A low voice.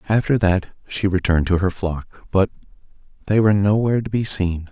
Yes: very low, 95 Hz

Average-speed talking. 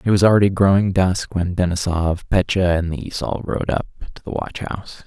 Yes: average, 190 wpm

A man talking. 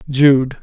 Yes: male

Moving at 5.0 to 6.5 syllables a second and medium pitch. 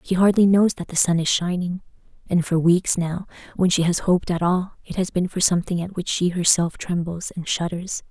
Yes: 5.4 syllables/s; medium, 175 Hz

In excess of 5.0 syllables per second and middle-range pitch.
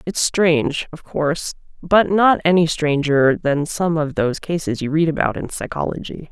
No: 4.8 syllables/s; medium, 155 Hz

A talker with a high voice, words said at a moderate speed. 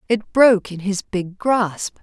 Yes: high, 205 Hz; average, 175 wpm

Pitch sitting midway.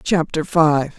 Yes: medium, 155 Hz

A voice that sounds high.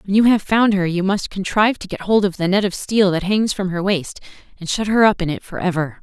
Yes: high, 195 Hz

